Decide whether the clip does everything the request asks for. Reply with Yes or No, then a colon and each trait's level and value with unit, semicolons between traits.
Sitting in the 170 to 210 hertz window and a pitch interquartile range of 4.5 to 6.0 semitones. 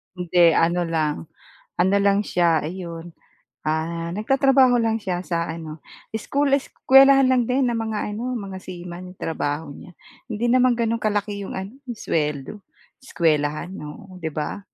Yes: medium, 185 Hz; wide, 5.6 semitones